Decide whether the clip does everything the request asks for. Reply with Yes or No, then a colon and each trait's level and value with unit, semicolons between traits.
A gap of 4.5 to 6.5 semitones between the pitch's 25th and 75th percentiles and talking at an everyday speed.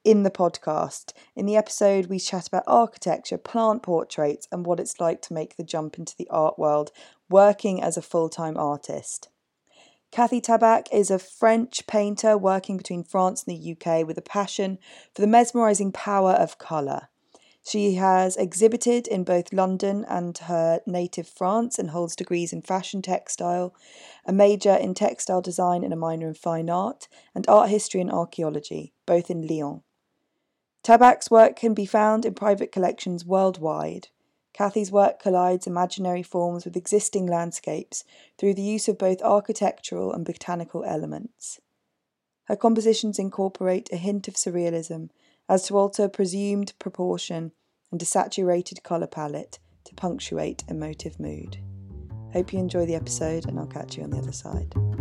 No: average, 3.3 semitones; average, 160 wpm